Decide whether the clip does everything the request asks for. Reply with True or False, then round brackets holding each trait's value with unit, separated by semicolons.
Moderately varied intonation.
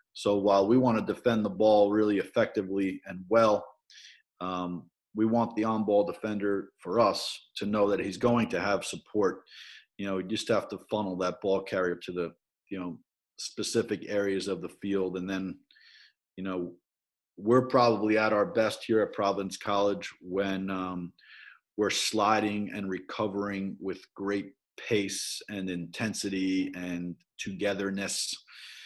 False (2.2 semitones)